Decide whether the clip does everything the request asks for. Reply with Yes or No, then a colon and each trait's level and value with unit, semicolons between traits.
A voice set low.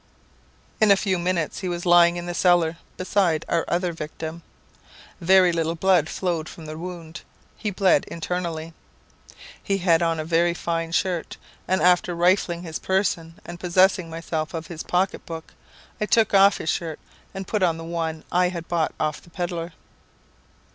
No: medium, 175 Hz